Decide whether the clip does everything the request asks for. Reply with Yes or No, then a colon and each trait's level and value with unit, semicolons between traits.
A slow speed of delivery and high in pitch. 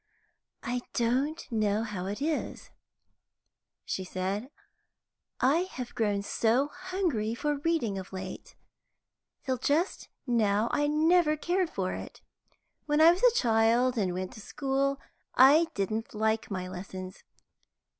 Yes: slow, 130 wpm; high, 240 Hz